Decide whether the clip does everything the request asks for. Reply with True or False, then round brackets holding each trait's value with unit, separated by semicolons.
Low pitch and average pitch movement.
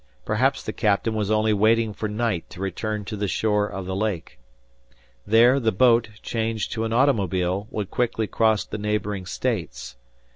False (105 Hz; 2.3 semitones)